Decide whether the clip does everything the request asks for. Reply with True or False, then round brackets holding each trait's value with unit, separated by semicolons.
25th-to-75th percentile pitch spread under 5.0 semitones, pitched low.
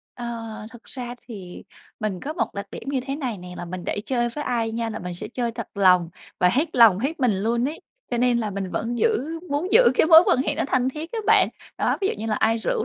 False (4.6 semitones; 235 Hz)